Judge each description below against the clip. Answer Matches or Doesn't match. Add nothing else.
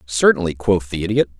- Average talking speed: Matches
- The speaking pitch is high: Doesn't match